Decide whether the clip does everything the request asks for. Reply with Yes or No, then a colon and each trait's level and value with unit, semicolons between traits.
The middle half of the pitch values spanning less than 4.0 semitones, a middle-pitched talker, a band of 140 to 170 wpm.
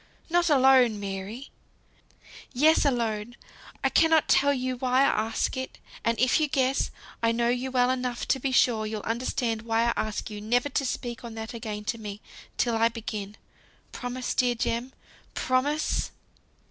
No: narrow, 2.6 semitones; high, 245 Hz; average, 165 wpm